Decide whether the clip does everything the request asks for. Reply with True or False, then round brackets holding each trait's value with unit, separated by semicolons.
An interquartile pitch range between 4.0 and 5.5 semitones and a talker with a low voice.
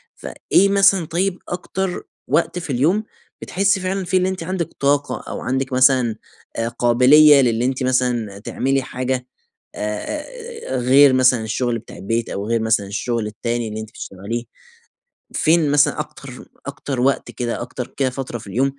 True (4.7 semitones; 130 Hz)